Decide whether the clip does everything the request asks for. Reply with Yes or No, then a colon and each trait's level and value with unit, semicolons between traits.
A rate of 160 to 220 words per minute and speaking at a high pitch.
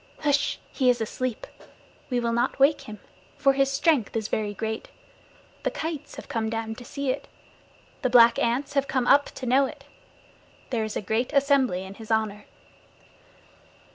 Yes: average, 170 wpm; high, 245 Hz